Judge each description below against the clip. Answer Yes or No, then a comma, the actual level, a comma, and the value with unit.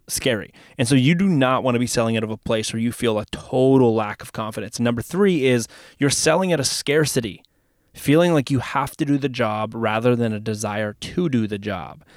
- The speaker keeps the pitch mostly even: No, average, 3.8 semitones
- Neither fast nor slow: No, fast, 225 wpm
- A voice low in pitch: Yes, low, 120 Hz